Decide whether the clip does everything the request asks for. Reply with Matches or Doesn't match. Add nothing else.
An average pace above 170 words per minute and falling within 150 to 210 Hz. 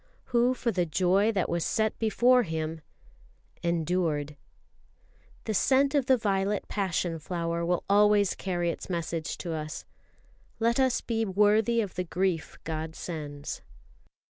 Doesn't match